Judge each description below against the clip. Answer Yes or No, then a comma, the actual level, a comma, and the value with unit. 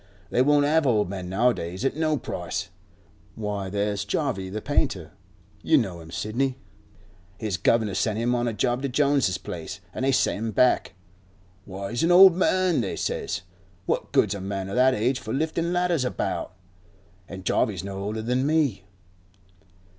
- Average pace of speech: Yes, average, 170 wpm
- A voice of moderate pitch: No, low, 115 Hz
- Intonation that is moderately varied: No, wide, 6.0 semitones